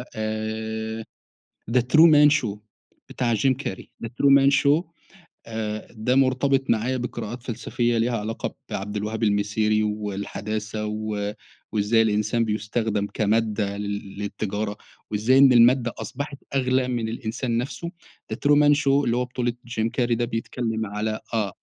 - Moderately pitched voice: No, low, 115 Hz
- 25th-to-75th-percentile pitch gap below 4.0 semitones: Yes, average, 2.8 semitones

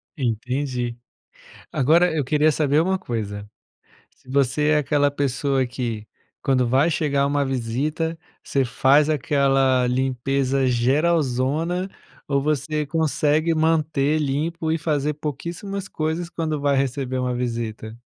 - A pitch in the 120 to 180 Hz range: Yes, medium, 140 Hz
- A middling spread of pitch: Yes, average, 3.3 semitones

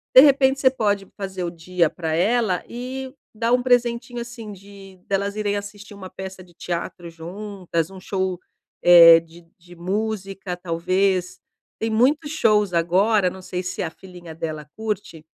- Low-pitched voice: No, high, 195 Hz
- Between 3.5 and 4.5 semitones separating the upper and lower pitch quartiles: Yes, average, 3.8 semitones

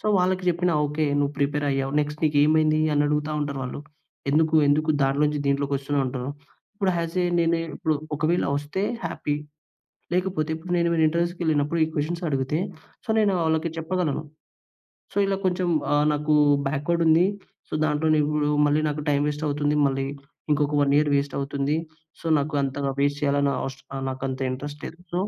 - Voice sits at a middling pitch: Yes, medium, 150 Hz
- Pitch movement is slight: Yes, narrow, 2.2 semitones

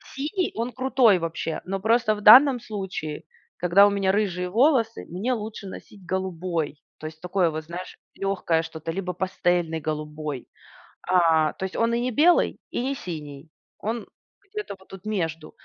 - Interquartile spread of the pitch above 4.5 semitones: Yes, average, 5.3 semitones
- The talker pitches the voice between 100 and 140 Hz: No, high, 190 Hz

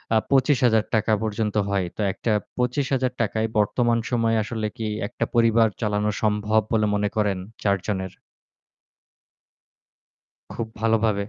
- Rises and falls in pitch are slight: Yes, narrow, 2.0 semitones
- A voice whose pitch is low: Yes, low, 110 Hz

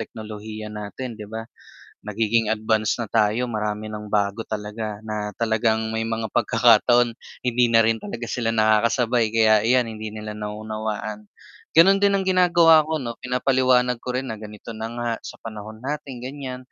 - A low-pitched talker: Yes, low, 110 Hz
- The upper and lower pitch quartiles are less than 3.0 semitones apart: Yes, narrow, 2.5 semitones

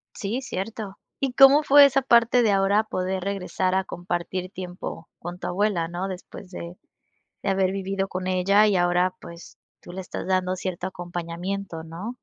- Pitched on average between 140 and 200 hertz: Yes, high, 190 Hz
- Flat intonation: Yes, narrow, 2.3 semitones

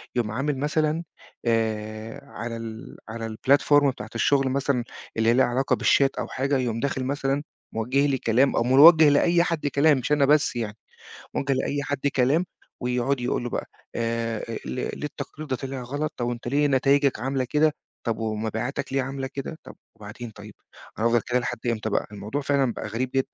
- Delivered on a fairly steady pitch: No, average, 3.5 semitones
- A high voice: No, low, 130 Hz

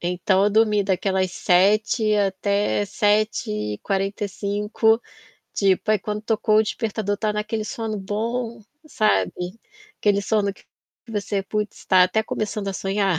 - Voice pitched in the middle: No, high, 205 Hz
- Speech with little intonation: Yes, narrow, 1.8 semitones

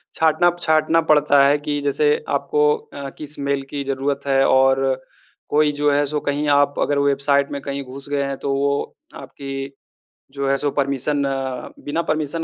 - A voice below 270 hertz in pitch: Yes, medium, 140 Hz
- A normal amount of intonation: No, narrow, 1.1 semitones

